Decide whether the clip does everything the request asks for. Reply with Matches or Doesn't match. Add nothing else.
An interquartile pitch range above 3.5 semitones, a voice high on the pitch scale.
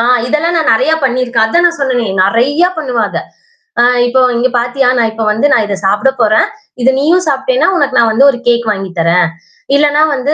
Matches